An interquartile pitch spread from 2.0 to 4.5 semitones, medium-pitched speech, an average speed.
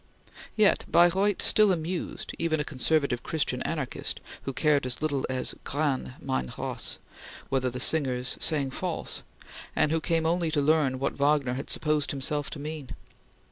Yes: average, 3.4 semitones; medium, 150 Hz; average, 155 wpm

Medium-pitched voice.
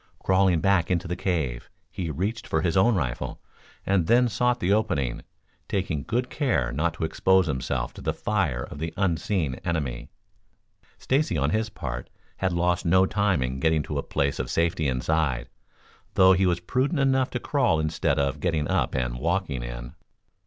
No: very low, 85 Hz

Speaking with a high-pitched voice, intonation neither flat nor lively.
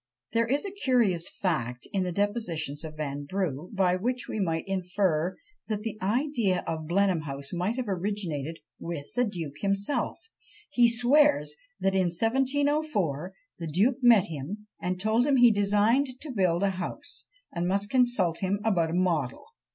No: high, 195 Hz; wide, 5.7 semitones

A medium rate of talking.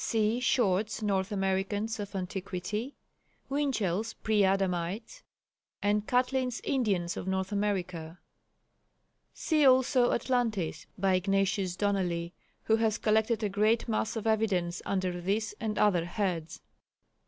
No: slow, 120 wpm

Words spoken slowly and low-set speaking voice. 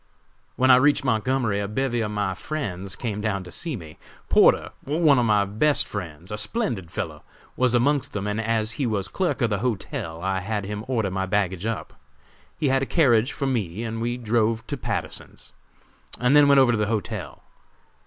No: average, 195 wpm; low, 110 Hz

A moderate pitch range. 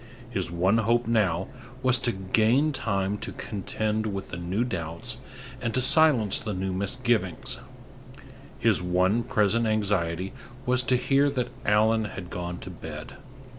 Yes: average, 4.1 semitones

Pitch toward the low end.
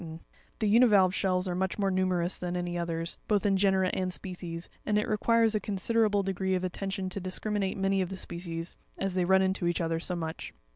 No: high, 190 Hz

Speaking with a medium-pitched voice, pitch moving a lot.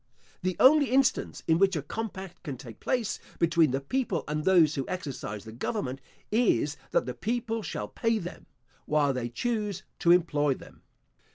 Yes: medium, 170 Hz; wide, 7.6 semitones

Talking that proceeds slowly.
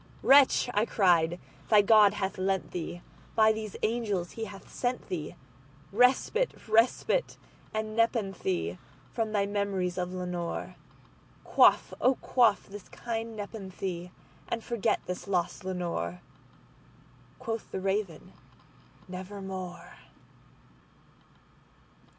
Yes: slow, 90 wpm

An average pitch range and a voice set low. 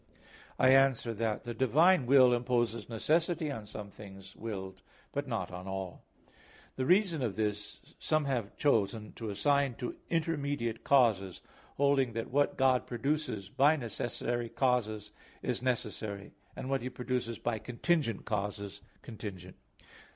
Yes: average, 4.5 semitones; low, 120 Hz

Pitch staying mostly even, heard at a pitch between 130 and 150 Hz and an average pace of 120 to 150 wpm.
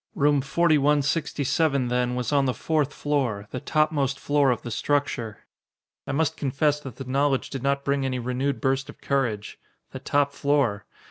No: narrow, 2.3 semitones; medium, 140 Hz; average, 165 wpm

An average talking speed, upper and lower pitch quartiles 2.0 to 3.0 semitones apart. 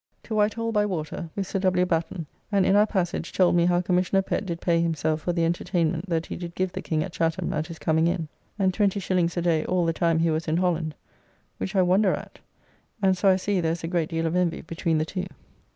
No: fast, 245 wpm; narrow, 2.4 semitones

